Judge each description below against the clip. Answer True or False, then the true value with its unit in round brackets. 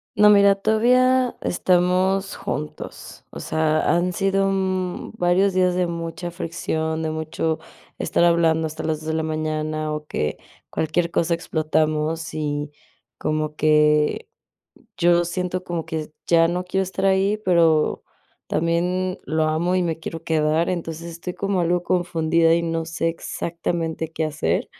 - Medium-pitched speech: True (170 Hz)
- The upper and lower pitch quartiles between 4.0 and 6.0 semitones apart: False (2.5 semitones)